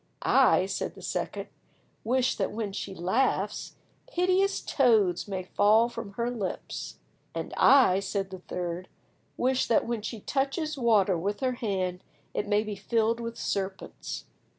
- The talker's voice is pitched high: Yes, high, 215 Hz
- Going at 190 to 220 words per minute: No, average, 150 wpm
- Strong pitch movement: No, average, 4.2 semitones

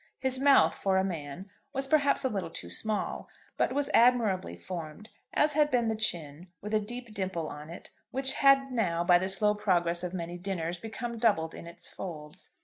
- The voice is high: Yes, high, 195 Hz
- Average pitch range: No, wide, 6.1 semitones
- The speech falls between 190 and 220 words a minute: Yes, average, 195 wpm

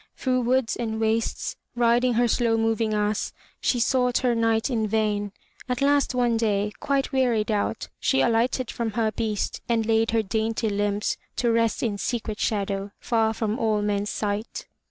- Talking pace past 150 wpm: Yes, average, 170 wpm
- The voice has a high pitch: Yes, high, 225 Hz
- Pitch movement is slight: Yes, narrow, 2.1 semitones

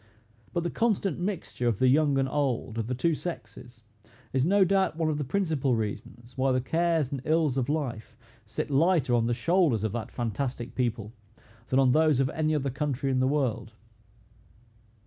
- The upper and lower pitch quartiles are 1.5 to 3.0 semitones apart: No, average, 4.7 semitones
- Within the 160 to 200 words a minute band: Yes, average, 185 wpm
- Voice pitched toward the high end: No, low, 135 Hz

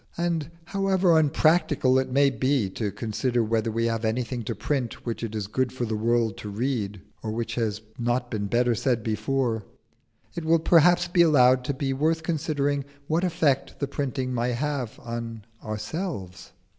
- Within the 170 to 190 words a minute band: Yes, average, 175 wpm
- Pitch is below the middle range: Yes, low, 125 Hz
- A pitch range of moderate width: Yes, average, 4.6 semitones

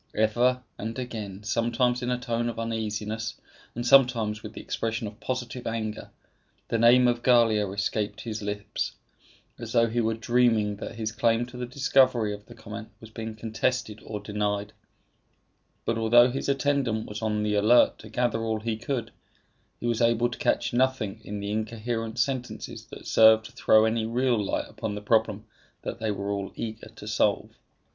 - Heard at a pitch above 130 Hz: No, low, 115 Hz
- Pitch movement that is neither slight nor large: No, narrow, 2.1 semitones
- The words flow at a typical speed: Yes, average, 180 wpm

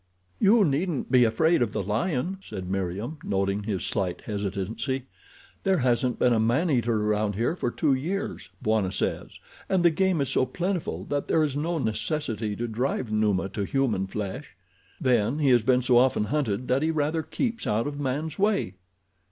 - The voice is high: No, low, 125 Hz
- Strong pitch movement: Yes, wide, 6.4 semitones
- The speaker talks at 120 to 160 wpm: No, average, 180 wpm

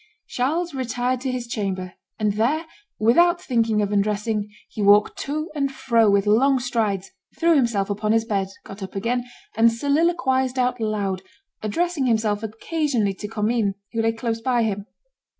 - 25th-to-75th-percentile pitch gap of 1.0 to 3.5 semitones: No, average, 3.9 semitones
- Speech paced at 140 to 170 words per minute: Yes, average, 160 wpm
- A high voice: Yes, high, 230 Hz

